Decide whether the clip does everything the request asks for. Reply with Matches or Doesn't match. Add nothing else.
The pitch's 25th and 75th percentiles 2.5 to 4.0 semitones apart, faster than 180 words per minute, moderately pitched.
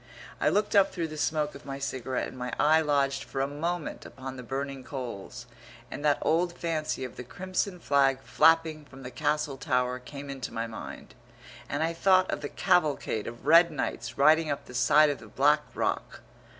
Matches